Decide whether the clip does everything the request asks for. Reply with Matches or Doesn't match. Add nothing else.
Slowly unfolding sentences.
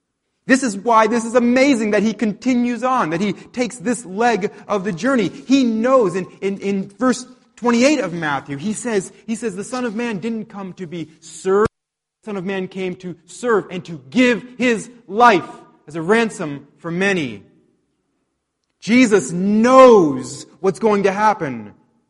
Doesn't match